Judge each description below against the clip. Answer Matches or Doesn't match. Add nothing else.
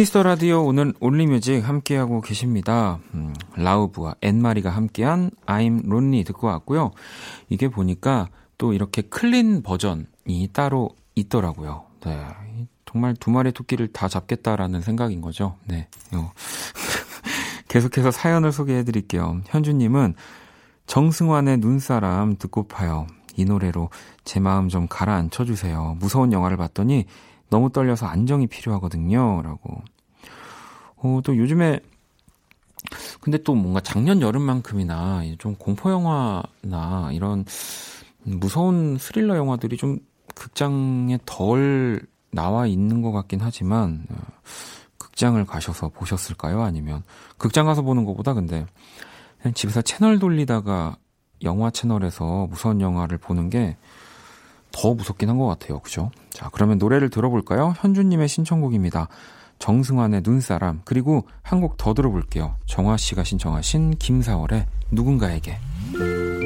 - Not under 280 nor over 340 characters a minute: Matches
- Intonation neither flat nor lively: Doesn't match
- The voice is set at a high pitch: Doesn't match